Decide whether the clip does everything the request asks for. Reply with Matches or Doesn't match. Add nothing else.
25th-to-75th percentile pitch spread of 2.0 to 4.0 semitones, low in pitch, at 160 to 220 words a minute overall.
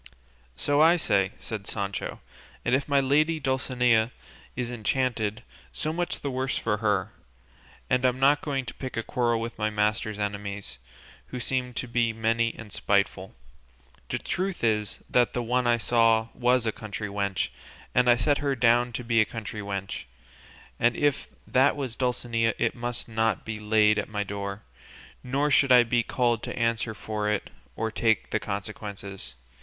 Matches